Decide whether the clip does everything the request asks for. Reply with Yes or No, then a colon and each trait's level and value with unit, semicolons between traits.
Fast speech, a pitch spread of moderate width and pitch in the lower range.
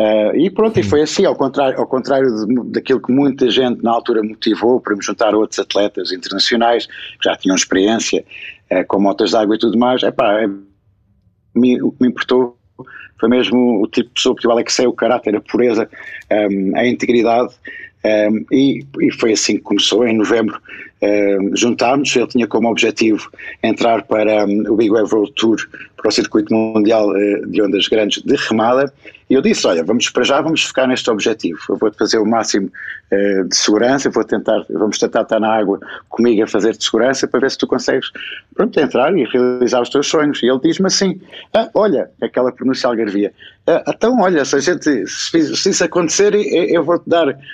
Yes: fast, 200 wpm; average, 4.7 semitones; low, 125 Hz